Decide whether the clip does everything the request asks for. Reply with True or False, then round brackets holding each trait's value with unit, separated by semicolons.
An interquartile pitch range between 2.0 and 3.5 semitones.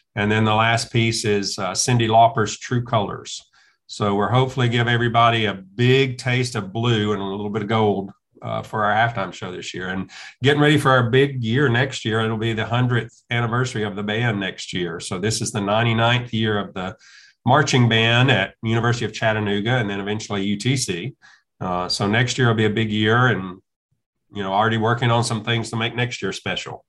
True (2.4 semitones)